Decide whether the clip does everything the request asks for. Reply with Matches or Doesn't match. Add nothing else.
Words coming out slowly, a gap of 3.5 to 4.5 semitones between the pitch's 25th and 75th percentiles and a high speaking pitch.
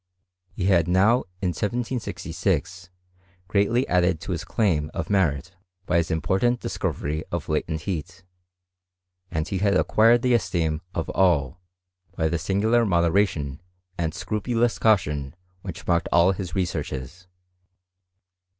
Doesn't match